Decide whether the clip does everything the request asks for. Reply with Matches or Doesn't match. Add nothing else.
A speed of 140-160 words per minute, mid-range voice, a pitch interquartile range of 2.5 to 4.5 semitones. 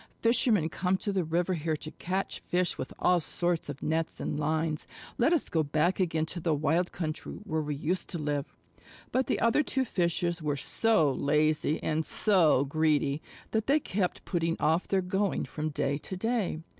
Doesn't match